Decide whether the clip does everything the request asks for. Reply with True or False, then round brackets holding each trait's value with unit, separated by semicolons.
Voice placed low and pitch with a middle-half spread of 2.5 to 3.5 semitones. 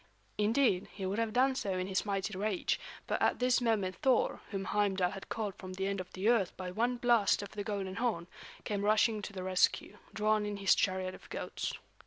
False (205 Hz; 2.8 semitones)